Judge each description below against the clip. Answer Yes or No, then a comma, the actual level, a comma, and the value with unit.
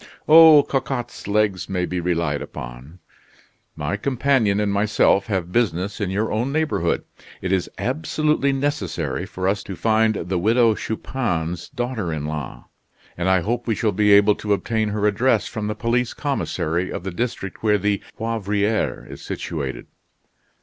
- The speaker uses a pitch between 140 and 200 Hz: No, low, 105 Hz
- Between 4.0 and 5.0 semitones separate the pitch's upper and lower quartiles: Yes, average, 4.3 semitones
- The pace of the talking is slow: No, average, 155 wpm